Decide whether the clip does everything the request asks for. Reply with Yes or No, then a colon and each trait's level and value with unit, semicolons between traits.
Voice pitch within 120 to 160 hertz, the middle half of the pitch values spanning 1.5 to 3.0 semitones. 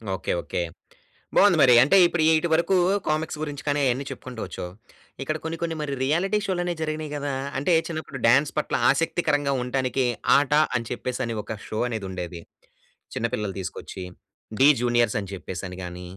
No: low, 135 Hz; average, 5.1 semitones